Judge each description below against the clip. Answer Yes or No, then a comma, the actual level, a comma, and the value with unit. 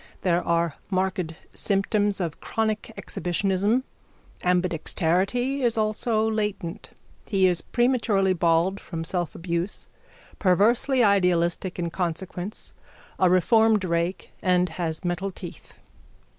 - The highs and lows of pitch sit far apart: No, average, 3.6 semitones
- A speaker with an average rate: No, slow, 105 wpm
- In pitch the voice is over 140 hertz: Yes, medium, 185 Hz